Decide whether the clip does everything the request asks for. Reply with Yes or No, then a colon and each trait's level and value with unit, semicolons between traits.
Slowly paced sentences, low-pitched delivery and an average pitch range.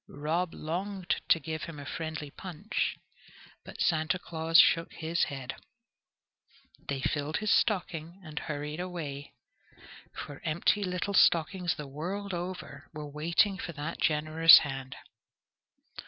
No: slow, 125 wpm; medium, 160 Hz; average, 3.0 semitones